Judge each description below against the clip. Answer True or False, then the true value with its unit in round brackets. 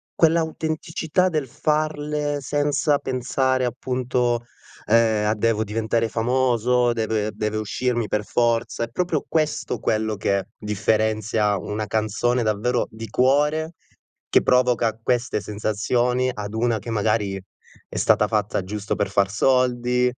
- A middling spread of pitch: True (3.3 semitones)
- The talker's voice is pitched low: True (120 Hz)